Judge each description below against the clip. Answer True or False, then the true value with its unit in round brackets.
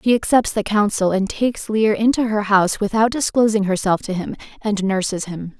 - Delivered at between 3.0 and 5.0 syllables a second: False (5.4 syllables/s)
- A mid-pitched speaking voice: False (210 Hz)